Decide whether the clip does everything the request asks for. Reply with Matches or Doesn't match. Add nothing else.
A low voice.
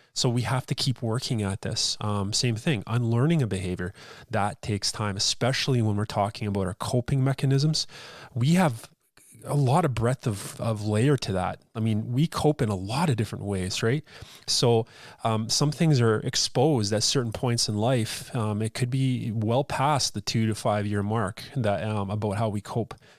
Matches